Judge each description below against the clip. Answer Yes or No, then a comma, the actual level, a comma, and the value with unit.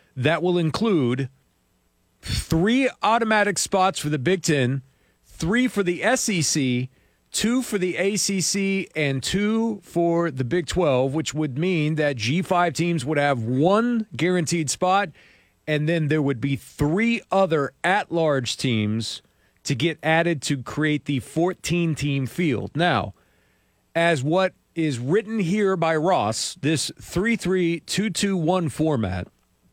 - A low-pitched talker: No, medium, 165 Hz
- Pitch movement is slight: No, average, 5.1 semitones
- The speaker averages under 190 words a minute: Yes, average, 140 wpm